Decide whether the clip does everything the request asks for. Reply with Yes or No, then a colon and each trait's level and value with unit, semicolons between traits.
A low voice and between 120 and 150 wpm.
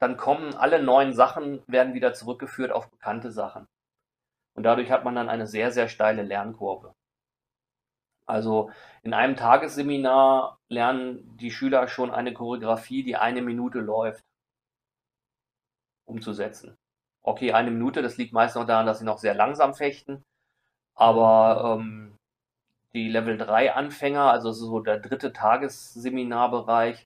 Yes: low, 120 Hz; average, 135 wpm